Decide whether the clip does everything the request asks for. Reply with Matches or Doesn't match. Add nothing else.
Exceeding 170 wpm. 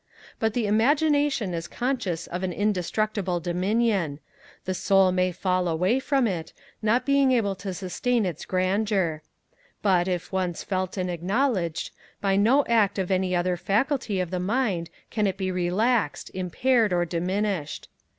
Doesn't match